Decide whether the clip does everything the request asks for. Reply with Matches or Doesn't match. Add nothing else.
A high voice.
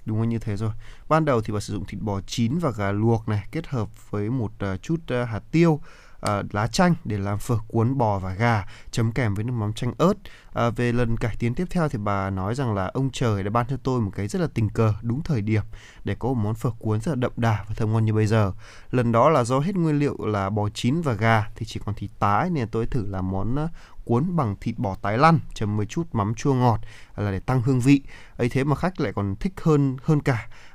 Doesn't match